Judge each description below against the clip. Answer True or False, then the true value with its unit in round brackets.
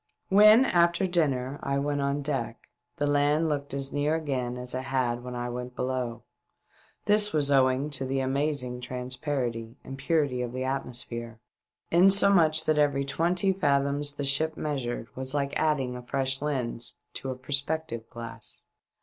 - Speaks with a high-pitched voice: False (140 Hz)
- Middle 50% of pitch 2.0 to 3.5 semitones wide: True (3.1 semitones)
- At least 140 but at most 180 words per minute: True (160 wpm)